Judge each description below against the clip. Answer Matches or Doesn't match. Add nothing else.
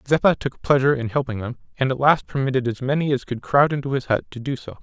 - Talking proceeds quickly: Matches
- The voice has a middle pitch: Doesn't match